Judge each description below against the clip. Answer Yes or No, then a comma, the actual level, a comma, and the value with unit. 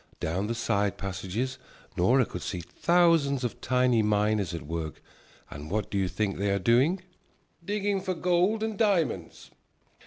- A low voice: Yes, low, 115 Hz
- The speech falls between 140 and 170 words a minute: Yes, average, 155 wpm